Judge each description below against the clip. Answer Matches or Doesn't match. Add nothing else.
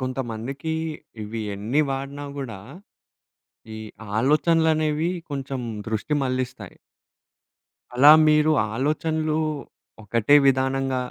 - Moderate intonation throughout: Matches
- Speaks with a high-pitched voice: Doesn't match